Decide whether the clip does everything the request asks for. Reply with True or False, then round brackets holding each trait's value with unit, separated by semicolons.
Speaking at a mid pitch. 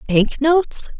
False (285 Hz)